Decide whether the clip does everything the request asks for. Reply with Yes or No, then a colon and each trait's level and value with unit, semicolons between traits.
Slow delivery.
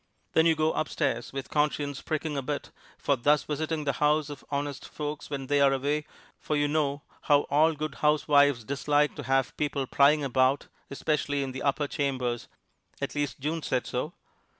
No: average, 180 wpm